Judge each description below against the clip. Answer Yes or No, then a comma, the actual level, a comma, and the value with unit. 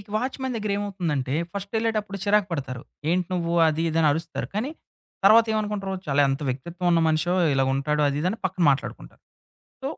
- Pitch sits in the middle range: Yes, medium, 175 Hz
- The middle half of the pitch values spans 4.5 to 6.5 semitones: Yes, wide, 5.6 semitones